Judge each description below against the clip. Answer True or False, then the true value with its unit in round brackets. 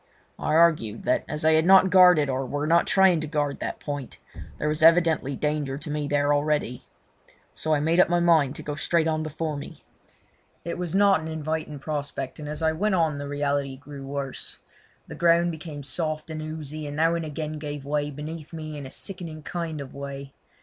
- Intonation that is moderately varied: False (2.2 semitones)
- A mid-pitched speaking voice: True (155 Hz)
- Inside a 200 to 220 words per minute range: True (205 wpm)